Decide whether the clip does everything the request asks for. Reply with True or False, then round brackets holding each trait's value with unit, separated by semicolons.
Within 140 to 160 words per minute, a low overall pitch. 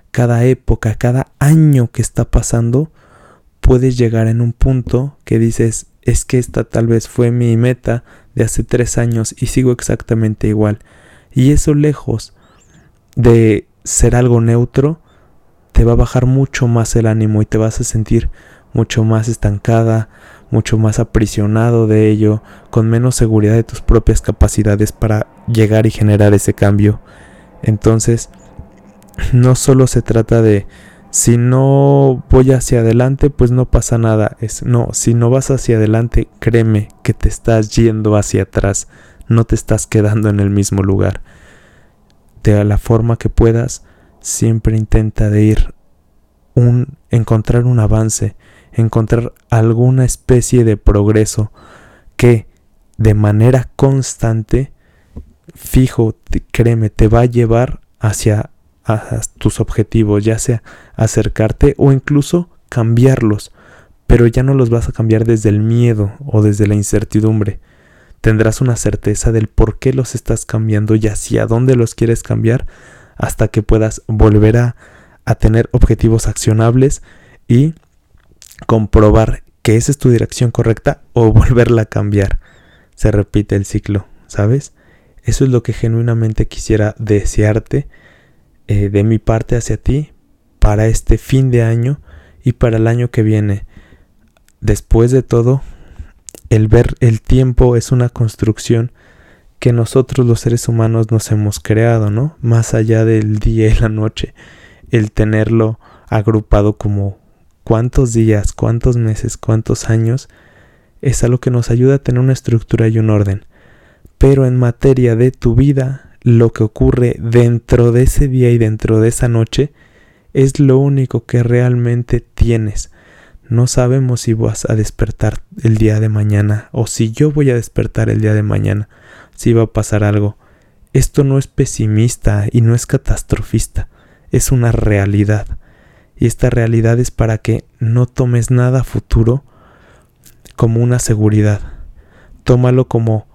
True (145 wpm; 115 Hz)